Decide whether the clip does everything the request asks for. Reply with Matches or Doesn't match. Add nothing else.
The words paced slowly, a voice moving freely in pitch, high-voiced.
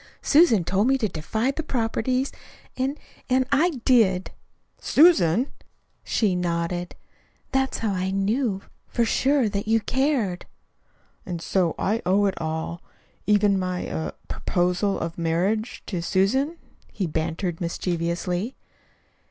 Matches